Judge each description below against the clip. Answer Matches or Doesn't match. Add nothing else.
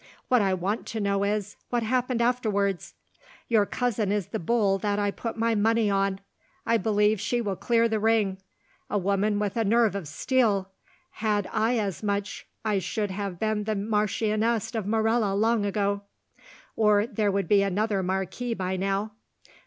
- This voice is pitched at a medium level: Doesn't match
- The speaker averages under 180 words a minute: Matches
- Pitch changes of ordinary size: Doesn't match